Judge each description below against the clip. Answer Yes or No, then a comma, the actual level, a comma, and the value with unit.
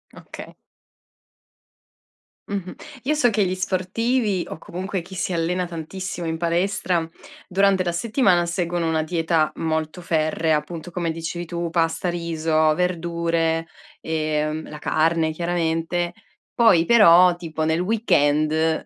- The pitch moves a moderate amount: No, narrow, 2.2 semitones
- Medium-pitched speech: Yes, medium, 170 Hz